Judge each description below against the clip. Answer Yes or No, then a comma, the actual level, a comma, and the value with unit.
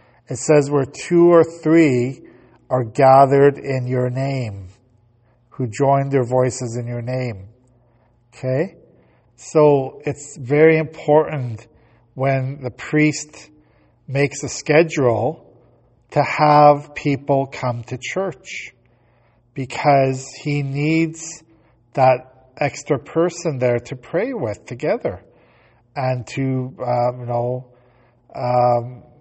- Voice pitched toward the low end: Yes, low, 130 Hz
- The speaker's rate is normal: No, slow, 105 wpm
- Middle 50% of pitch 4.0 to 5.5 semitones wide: No, average, 3.3 semitones